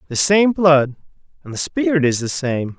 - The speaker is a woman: No, male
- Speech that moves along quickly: No, average, 195 wpm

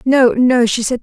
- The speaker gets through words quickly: Yes, fast, 235 wpm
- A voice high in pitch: Yes, high, 245 Hz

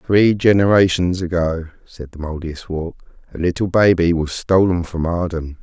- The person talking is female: No, male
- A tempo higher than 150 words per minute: No, average, 140 wpm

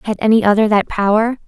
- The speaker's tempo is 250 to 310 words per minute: No, fast, 205 wpm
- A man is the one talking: No, female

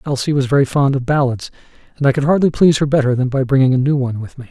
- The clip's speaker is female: No, male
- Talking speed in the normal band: No, fast, 280 wpm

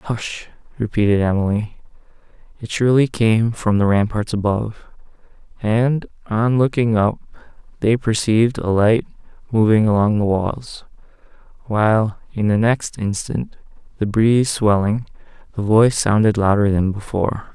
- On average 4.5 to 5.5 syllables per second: Yes, 4.7 syllables/s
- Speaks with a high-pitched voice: No, low, 110 Hz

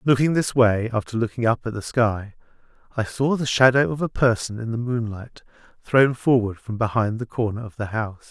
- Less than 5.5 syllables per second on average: Yes, 5.3 syllables/s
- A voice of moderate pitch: No, low, 115 Hz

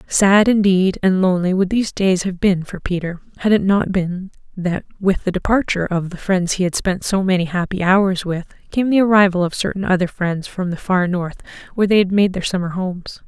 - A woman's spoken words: Yes, female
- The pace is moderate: No, fast, 215 wpm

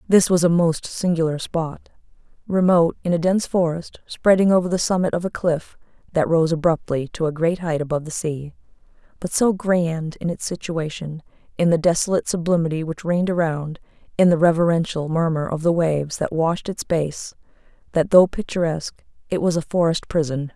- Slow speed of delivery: No, average, 175 wpm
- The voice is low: No, medium, 165 Hz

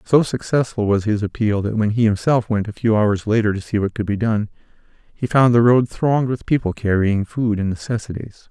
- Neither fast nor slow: No, fast, 220 wpm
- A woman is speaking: No, male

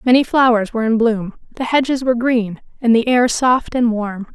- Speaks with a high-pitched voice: Yes, high, 235 Hz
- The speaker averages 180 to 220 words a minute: Yes, fast, 205 wpm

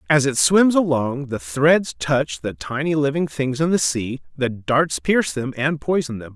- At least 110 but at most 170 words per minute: No, average, 200 wpm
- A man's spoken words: Yes, male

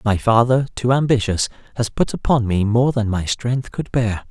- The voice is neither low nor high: No, low, 115 Hz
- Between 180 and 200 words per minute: Yes, average, 195 wpm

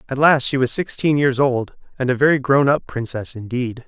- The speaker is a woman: No, male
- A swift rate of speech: Yes, fast, 215 wpm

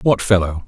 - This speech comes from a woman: No, male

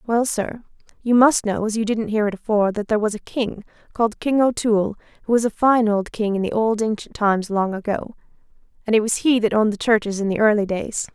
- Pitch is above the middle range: Yes, high, 215 Hz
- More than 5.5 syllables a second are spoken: Yes, 6.0 syllables/s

